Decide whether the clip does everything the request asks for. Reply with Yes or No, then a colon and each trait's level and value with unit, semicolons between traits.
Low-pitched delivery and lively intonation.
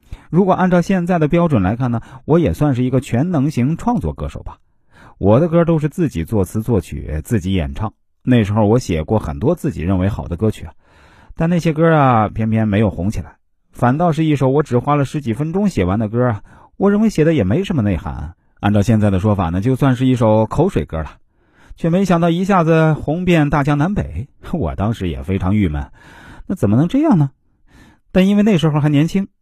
Yes: low, 125 Hz; wide, 8.6 semitones